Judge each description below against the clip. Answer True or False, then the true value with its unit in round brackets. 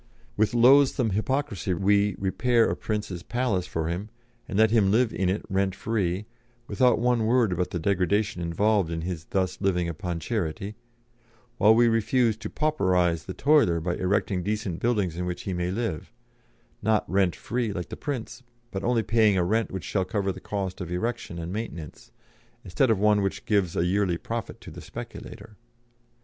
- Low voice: True (100 Hz)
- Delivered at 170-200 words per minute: True (180 wpm)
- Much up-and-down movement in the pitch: False (3.9 semitones)